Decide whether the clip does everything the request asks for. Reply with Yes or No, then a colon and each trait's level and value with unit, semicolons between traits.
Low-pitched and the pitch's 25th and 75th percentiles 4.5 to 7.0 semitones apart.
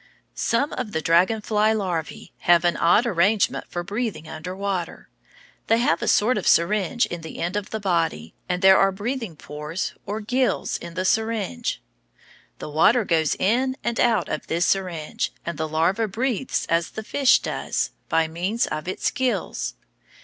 No: high, 190 Hz; average, 4.8 semitones